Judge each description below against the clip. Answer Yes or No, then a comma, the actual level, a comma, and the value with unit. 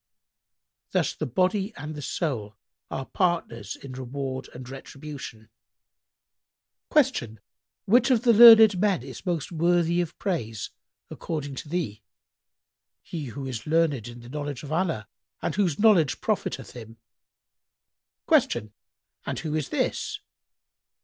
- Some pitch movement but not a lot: No, wide, 6.1 semitones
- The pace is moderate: No, slow, 125 wpm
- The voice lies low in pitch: No, medium, 150 Hz